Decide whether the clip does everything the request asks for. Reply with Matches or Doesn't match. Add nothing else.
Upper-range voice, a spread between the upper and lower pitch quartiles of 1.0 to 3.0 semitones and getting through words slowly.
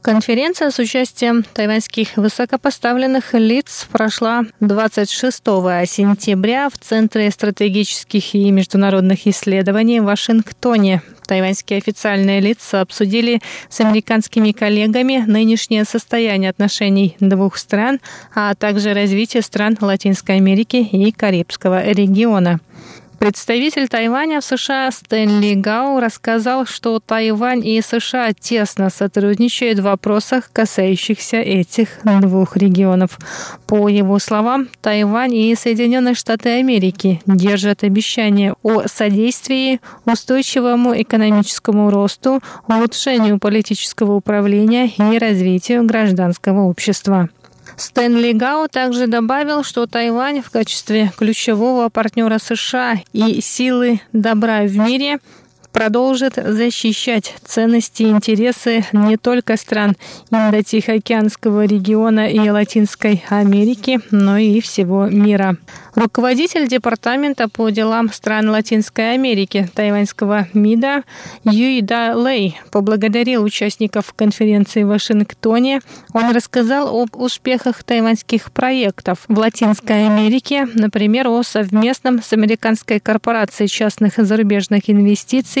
Matches